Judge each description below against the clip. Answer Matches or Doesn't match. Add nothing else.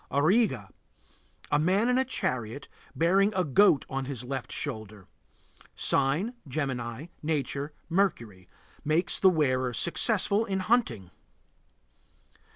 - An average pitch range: Doesn't match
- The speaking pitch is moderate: Matches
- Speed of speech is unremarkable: Doesn't match